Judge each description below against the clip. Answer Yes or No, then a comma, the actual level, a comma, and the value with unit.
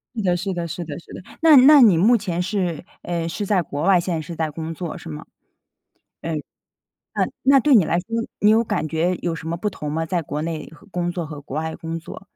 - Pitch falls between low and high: Yes, medium, 170 Hz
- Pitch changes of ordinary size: Yes, average, 3.3 semitones